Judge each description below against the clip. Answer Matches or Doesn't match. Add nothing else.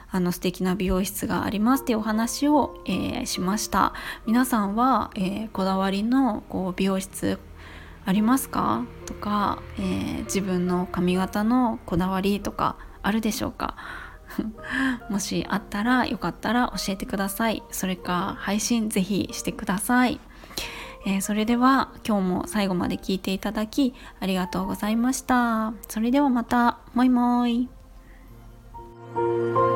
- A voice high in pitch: Matches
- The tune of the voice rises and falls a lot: Doesn't match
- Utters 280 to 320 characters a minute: Matches